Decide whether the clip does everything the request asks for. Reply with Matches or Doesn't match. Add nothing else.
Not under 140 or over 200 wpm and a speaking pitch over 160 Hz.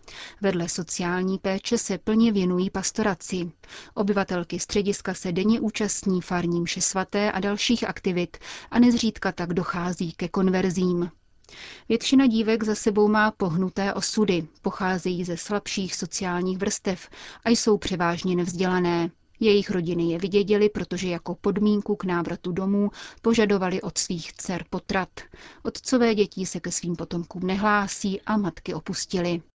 Doesn't match